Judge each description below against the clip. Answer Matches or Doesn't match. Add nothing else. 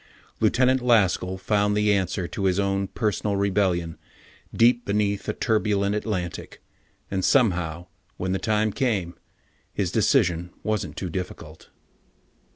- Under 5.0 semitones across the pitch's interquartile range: Matches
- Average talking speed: Doesn't match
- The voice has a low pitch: Matches